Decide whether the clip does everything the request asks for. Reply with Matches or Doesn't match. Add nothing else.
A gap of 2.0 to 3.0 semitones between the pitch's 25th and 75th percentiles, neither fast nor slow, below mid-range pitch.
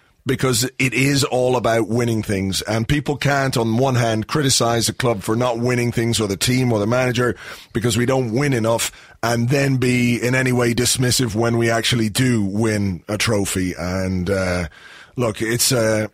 Matches